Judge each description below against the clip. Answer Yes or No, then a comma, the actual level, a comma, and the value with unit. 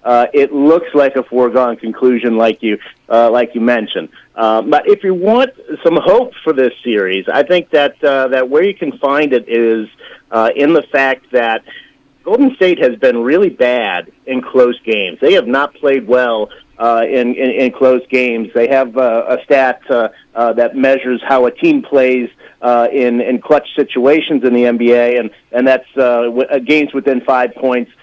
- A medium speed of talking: Yes, average, 190 wpm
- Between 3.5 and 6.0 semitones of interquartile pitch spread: No, average, 2.9 semitones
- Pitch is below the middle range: Yes, low, 130 Hz